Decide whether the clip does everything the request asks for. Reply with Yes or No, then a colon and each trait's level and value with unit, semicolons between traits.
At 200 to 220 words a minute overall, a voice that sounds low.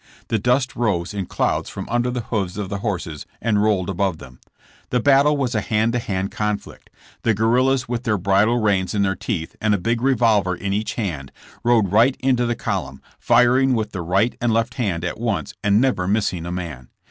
Yes: fast, 205 wpm; low, 105 Hz